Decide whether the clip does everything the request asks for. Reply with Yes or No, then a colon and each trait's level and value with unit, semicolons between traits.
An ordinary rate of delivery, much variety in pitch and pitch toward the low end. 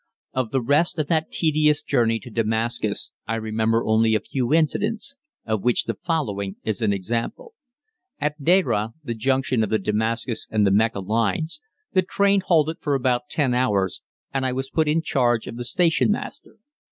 Yes: average, 175 wpm; wide, 5.7 semitones; low, 125 Hz